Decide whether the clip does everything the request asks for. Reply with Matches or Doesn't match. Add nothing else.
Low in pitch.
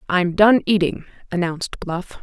Doesn't match